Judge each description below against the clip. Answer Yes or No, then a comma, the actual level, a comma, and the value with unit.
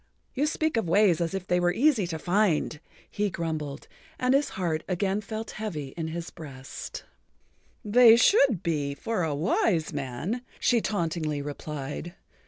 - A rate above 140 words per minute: Yes, average, 150 wpm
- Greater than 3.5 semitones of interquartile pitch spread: Yes, wide, 5.6 semitones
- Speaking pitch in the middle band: Yes, medium, 175 Hz